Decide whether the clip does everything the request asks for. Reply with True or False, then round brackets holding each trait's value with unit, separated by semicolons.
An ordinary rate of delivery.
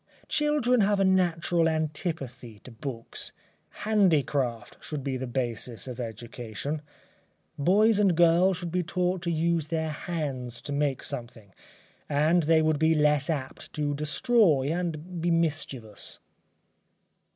False (130 wpm)